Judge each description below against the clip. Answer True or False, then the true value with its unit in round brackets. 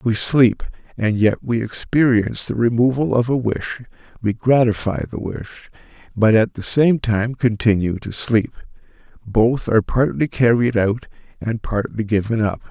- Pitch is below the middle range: True (115 Hz)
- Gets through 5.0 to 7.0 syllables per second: False (4.6 syllables/s)